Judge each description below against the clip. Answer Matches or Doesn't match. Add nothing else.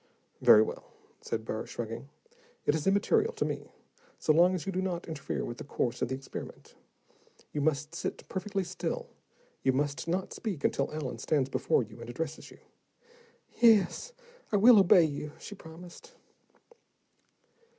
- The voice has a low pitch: Doesn't match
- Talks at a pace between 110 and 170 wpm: Matches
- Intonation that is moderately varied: Doesn't match